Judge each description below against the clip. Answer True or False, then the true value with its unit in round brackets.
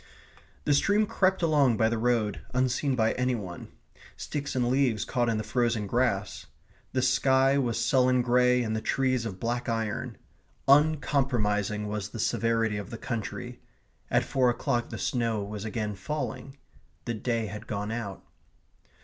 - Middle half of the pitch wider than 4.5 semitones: False (3.2 semitones)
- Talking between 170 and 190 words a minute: False (160 wpm)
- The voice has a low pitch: True (120 Hz)